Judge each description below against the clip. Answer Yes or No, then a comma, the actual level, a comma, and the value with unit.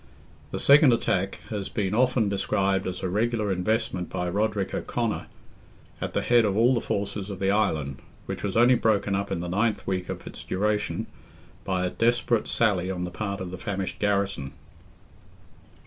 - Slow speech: No, average, 180 wpm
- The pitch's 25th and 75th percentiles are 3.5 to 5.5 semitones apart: No, average, 2.9 semitones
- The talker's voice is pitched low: Yes, low, 100 Hz